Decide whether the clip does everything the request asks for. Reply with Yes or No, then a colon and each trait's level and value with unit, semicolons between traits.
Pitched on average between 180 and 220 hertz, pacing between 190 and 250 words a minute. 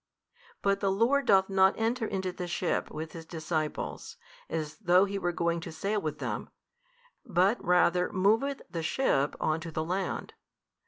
No: medium, 185 Hz; average, 165 wpm